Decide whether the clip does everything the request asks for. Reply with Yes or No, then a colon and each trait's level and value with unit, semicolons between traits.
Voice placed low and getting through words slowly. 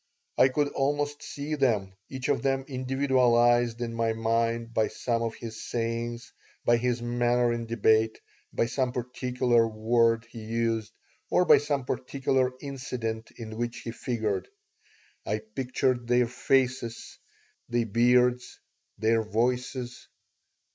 Yes: low, 120 Hz; slow, 130 wpm